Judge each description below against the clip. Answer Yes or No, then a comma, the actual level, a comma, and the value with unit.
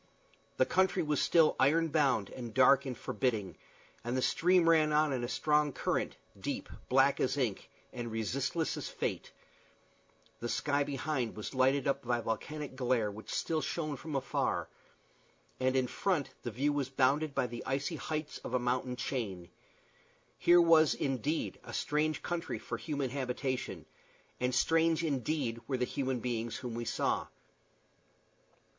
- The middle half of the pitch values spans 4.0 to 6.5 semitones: No, average, 3.6 semitones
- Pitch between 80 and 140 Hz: Yes, low, 135 Hz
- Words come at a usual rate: Yes, average, 160 wpm